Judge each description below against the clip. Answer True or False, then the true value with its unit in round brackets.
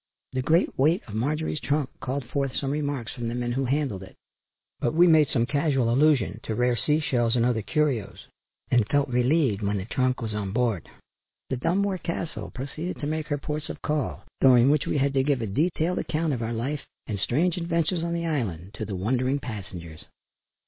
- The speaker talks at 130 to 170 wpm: False (205 wpm)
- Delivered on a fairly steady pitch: False (4.6 semitones)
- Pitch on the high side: False (135 Hz)